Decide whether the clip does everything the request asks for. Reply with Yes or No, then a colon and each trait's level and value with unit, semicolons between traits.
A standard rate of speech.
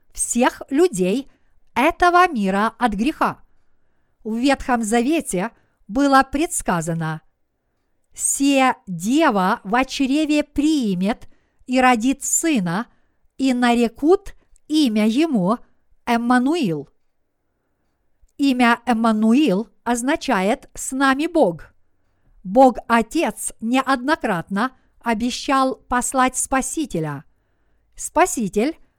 No: slow, 75 wpm